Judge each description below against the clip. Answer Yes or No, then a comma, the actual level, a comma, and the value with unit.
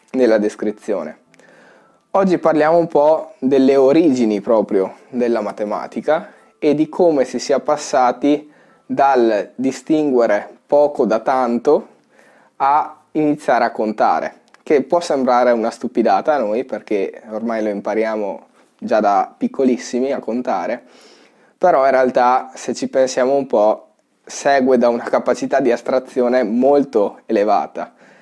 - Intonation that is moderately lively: Yes, average, 3.8 semitones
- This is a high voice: No, low, 130 Hz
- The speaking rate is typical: Yes, average, 125 wpm